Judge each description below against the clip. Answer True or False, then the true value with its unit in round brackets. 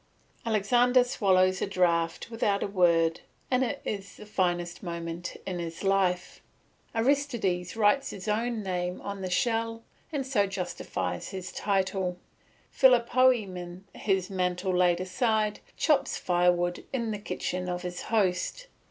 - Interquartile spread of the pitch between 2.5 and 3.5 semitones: False (4.1 semitones)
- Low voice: False (195 Hz)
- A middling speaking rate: False (130 wpm)